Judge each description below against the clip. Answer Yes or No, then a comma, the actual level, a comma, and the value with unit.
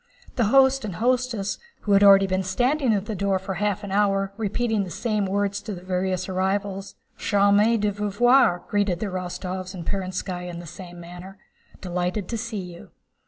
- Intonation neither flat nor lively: No, narrow, 2.2 semitones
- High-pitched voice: Yes, high, 195 Hz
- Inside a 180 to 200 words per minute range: Yes, average, 195 wpm